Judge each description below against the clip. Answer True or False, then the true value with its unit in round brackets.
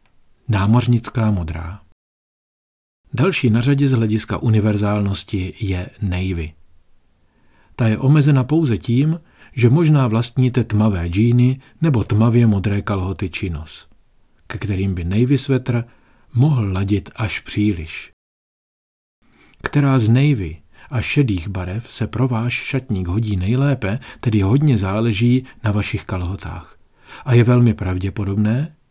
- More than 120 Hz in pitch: False (110 Hz)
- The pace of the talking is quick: False (115 wpm)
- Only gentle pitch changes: False (4.7 semitones)